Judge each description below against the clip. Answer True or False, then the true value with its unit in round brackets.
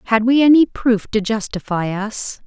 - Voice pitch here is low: False (225 Hz)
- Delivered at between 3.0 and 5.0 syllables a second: True (4.6 syllables/s)